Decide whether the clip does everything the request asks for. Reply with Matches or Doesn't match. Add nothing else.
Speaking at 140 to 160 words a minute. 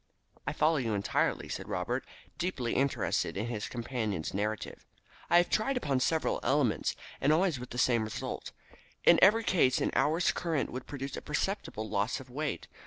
Doesn't match